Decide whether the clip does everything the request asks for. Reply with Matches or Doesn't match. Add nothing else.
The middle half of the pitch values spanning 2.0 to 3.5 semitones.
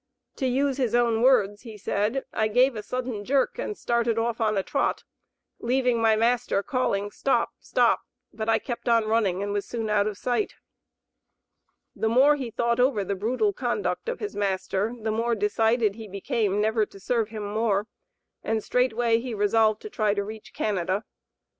Matches